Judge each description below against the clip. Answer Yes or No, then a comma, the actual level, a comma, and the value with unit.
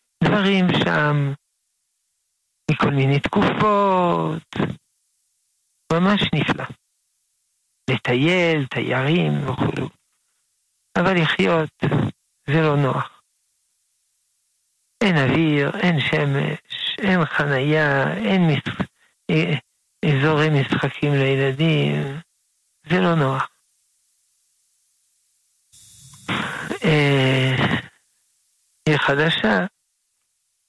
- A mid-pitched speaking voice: Yes, medium, 150 Hz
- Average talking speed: No, slow, 65 wpm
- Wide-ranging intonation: No, average, 3.6 semitones